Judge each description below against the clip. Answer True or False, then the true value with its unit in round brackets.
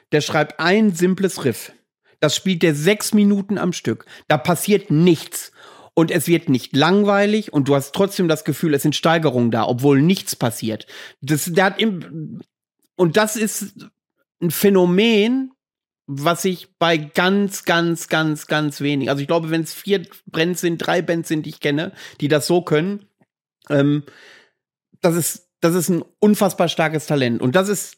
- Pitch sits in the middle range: True (170 Hz)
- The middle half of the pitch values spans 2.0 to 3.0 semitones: False (4.4 semitones)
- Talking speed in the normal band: True (170 wpm)